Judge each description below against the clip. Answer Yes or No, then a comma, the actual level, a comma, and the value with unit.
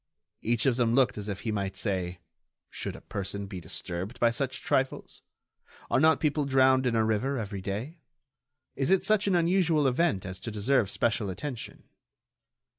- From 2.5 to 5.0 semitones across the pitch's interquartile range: No, wide, 5.6 semitones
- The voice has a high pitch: No, low, 120 Hz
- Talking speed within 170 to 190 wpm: Yes, average, 175 wpm